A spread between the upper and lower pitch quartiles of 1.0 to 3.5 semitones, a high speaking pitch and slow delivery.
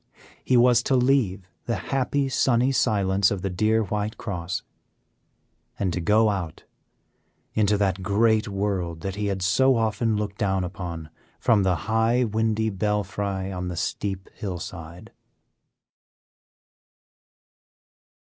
No: average, 2.9 semitones; low, 100 Hz; slow, 125 wpm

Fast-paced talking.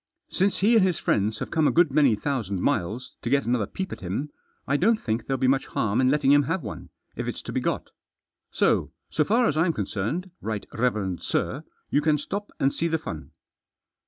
Yes: fast, 220 wpm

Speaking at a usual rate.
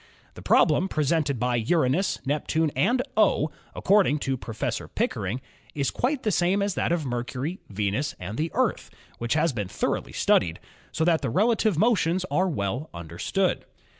Yes: average, 165 wpm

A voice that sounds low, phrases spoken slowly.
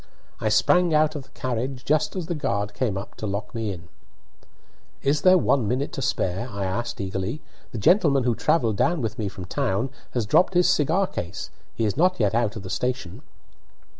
No: low, 120 Hz; average, 200 wpm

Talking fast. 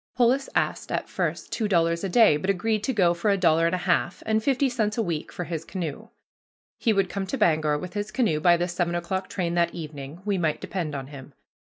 Yes: fast, 235 wpm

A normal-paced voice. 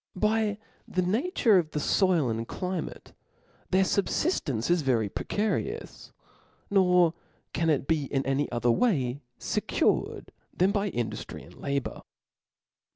No: slow, 125 wpm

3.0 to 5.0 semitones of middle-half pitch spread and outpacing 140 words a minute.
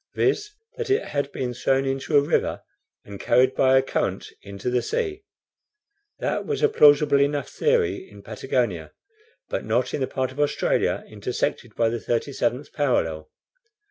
Yes: average, 3.3 semitones; average, 160 wpm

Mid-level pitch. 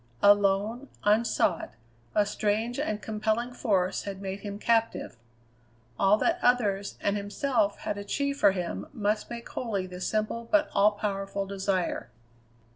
No: high, 205 Hz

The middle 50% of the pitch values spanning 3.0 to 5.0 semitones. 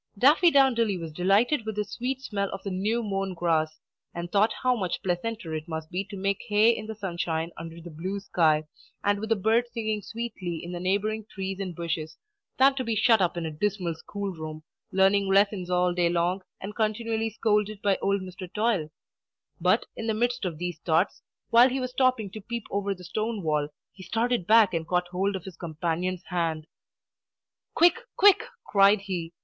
Yes: average, 4.1 semitones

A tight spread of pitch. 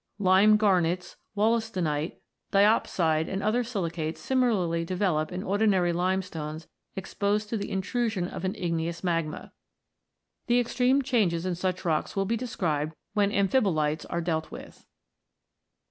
No: average, 4.1 semitones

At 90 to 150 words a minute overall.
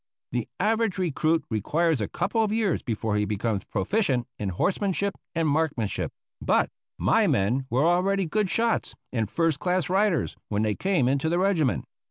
No: average, 165 wpm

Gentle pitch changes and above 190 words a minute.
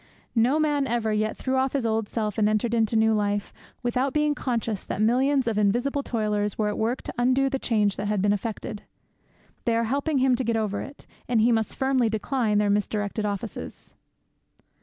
No: average, 3.6 semitones; average, 200 wpm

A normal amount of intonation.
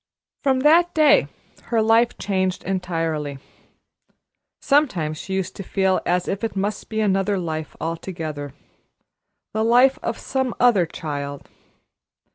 No: wide, 5.8 semitones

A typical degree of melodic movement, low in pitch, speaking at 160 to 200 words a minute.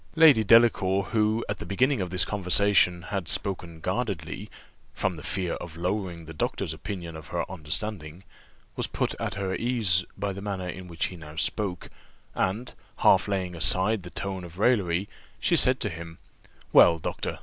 Yes: average, 3.2 semitones; very low, 95 Hz; average, 170 wpm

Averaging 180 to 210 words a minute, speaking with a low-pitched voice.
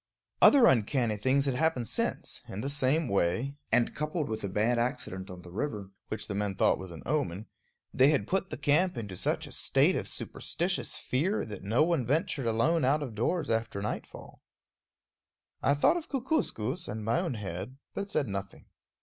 Yes: average, 185 wpm; low, 125 Hz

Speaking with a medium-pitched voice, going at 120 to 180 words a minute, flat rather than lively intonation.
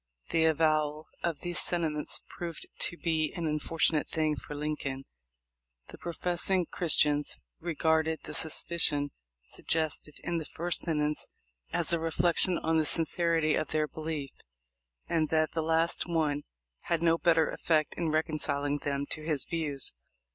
Yes: medium, 160 Hz; average, 140 wpm; narrow, 1.7 semitones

